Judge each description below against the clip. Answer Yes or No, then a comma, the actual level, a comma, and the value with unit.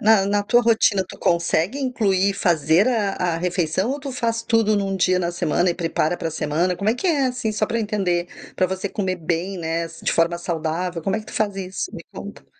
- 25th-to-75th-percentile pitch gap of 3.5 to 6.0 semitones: Yes, average, 4.1 semitones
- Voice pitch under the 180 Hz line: No, high, 190 Hz